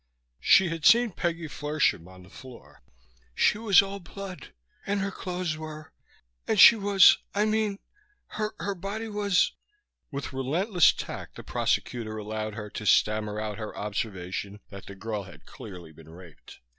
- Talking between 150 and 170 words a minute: Yes, average, 160 wpm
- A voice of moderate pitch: Yes, medium, 150 Hz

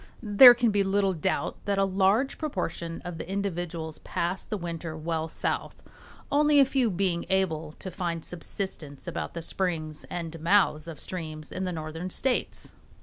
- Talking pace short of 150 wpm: No, average, 165 wpm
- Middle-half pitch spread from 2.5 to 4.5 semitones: Yes, average, 3.5 semitones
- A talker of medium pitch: Yes, medium, 180 Hz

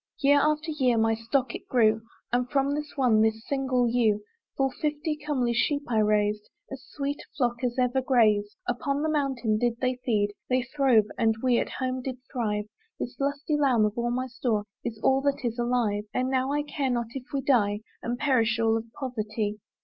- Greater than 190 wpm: Yes, average, 200 wpm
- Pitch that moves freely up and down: No, average, 3.5 semitones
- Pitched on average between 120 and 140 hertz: No, high, 245 Hz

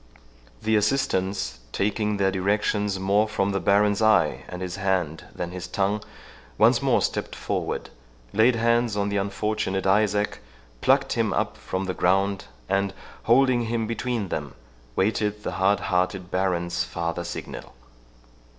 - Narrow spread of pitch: Yes, narrow, 2.2 semitones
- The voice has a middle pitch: No, low, 100 Hz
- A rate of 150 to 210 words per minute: No, average, 140 wpm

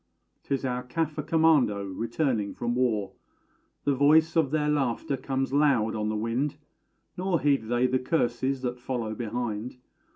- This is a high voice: No, low, 130 Hz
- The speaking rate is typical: Yes, average, 150 wpm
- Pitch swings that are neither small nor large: Yes, average, 4.0 semitones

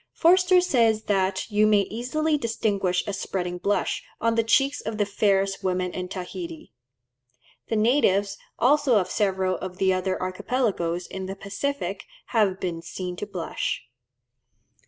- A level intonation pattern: No, average, 3.7 semitones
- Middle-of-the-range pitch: No, high, 200 Hz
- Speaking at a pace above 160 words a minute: No, average, 145 wpm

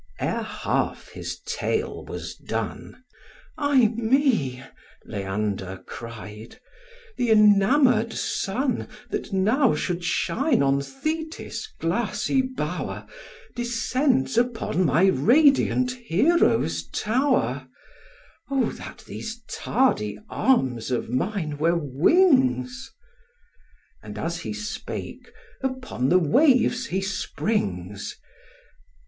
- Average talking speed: No, slow, 95 wpm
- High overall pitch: Yes, high, 215 Hz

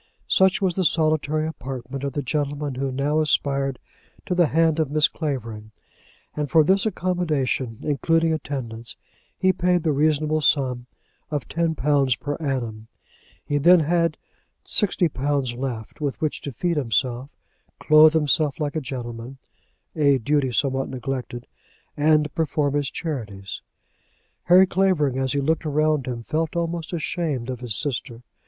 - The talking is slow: No, average, 145 wpm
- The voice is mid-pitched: Yes, medium, 145 Hz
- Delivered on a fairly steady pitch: No, average, 3.4 semitones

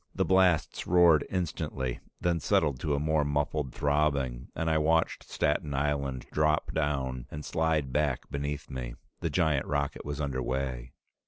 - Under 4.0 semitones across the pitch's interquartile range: Yes, narrow, 2.5 semitones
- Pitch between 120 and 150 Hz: No, very low, 75 Hz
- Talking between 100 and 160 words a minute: Yes, average, 155 wpm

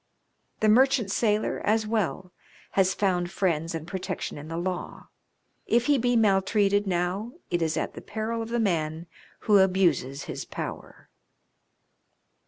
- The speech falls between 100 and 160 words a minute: Yes, average, 150 wpm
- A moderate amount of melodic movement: Yes, average, 4.0 semitones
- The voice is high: Yes, high, 195 Hz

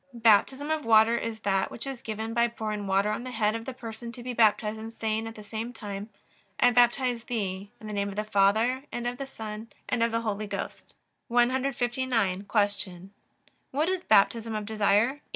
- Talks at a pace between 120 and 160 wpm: No, average, 200 wpm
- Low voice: No, high, 225 Hz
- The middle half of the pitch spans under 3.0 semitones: Yes, narrow, 2.5 semitones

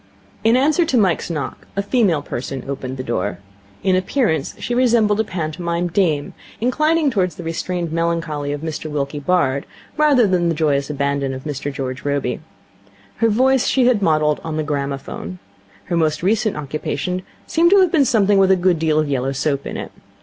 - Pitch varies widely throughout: Yes, wide, 6.8 semitones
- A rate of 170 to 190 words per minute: Yes, average, 185 wpm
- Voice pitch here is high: No, medium, 165 Hz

